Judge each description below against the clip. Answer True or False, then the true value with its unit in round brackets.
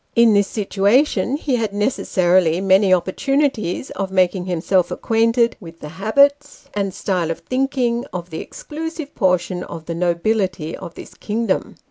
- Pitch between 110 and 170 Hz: False (195 Hz)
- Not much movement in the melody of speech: False (4.7 semitones)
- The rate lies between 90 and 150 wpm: True (145 wpm)